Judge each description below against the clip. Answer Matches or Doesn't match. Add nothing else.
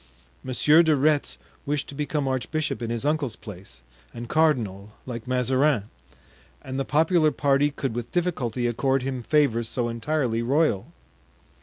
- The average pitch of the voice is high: Doesn't match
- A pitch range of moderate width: Matches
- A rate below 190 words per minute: Matches